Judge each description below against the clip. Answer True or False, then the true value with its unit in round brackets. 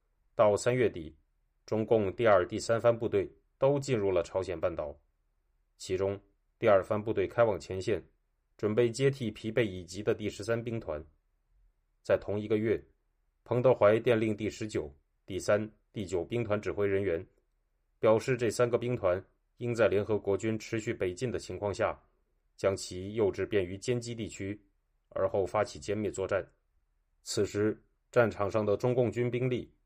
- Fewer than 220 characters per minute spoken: False (240 characters per minute)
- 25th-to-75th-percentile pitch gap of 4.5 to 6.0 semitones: True (5.3 semitones)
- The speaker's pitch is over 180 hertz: False (105 Hz)